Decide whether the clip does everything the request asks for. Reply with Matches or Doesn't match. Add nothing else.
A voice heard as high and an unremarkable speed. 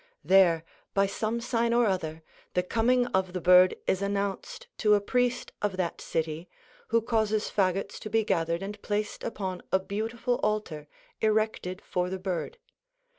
Matches